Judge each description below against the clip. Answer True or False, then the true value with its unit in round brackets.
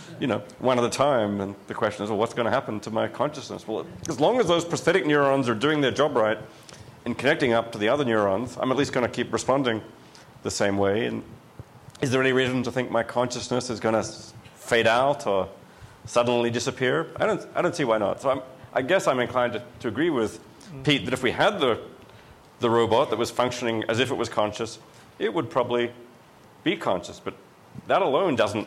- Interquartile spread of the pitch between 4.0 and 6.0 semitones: False (2.7 semitones)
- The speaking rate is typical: False (220 wpm)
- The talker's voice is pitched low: True (120 Hz)